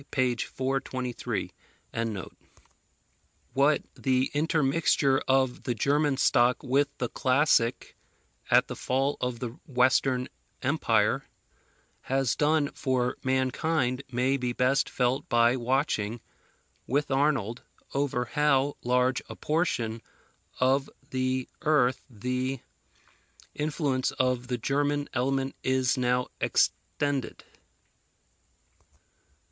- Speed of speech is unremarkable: No, slow, 100 wpm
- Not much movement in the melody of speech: Yes, narrow, 1.9 semitones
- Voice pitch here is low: Yes, low, 130 Hz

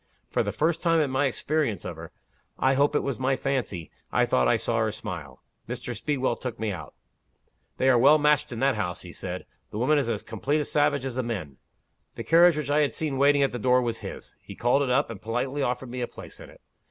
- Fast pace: Yes, fast, 245 wpm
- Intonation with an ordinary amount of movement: Yes, average, 4.1 semitones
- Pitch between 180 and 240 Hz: No, low, 130 Hz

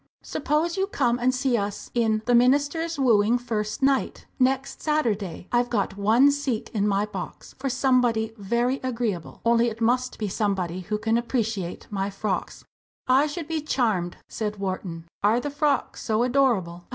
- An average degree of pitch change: Yes, average, 4.3 semitones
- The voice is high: Yes, high, 235 Hz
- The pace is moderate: Yes, average, 165 wpm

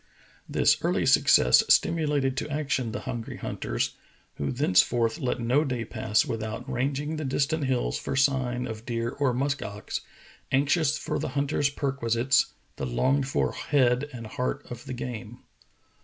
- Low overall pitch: Yes, low, 130 Hz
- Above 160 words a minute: No, average, 155 wpm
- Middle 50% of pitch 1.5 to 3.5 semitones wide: Yes, average, 3.2 semitones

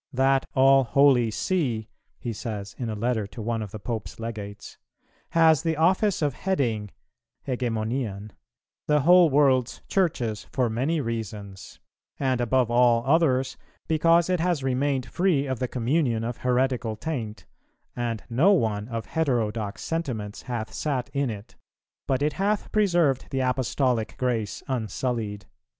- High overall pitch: No, low, 125 Hz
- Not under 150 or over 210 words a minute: No, average, 140 wpm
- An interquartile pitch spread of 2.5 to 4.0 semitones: No, average, 4.4 semitones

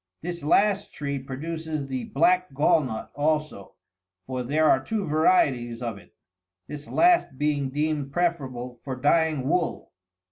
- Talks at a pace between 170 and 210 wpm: No, average, 150 wpm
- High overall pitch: No, medium, 145 Hz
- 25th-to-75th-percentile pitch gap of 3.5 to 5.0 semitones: Yes, average, 3.9 semitones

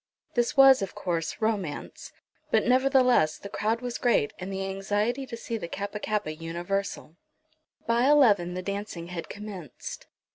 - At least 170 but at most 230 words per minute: No, average, 150 wpm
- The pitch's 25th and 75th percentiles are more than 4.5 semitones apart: Yes, average, 4.9 semitones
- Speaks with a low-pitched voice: No, high, 205 Hz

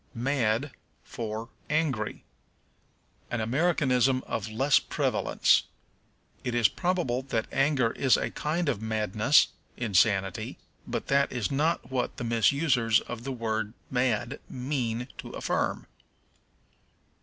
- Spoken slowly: Yes, slow, 115 wpm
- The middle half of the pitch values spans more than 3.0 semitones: Yes, average, 3.7 semitones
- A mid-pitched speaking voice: No, low, 125 Hz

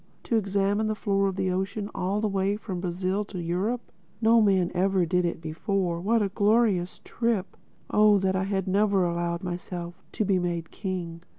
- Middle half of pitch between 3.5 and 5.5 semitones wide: No, narrow, 2.5 semitones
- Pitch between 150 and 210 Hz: Yes, high, 190 Hz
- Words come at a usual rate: Yes, average, 180 wpm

